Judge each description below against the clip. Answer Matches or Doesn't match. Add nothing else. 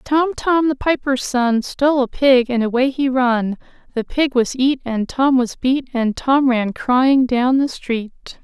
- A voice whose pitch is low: Doesn't match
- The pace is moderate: Matches